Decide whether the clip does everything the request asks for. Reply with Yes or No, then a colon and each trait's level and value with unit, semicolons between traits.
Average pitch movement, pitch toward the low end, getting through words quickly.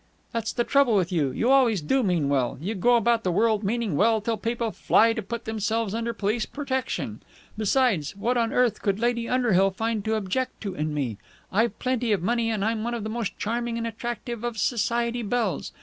No: average, 3.1 semitones; high, 225 Hz; fast, 210 wpm